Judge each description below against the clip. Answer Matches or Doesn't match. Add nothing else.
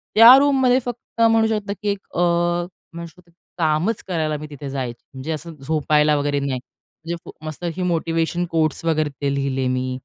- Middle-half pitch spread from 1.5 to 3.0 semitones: Doesn't match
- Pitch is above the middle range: Doesn't match